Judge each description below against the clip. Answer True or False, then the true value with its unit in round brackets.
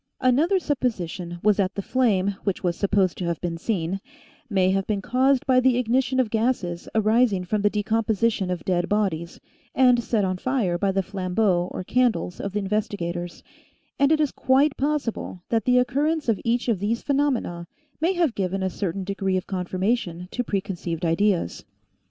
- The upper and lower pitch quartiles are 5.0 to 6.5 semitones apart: True (5.3 semitones)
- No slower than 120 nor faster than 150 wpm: False (180 wpm)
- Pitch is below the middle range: False (205 Hz)